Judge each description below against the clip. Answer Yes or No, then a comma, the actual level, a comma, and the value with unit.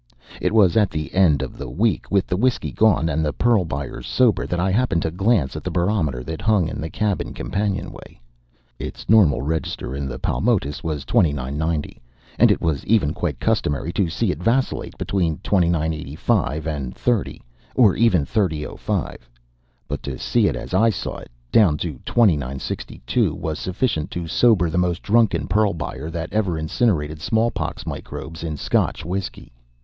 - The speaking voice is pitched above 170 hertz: No, very low, 85 Hz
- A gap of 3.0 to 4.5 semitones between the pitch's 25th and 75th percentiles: No, average, 5.3 semitones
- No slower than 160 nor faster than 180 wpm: Yes, average, 165 wpm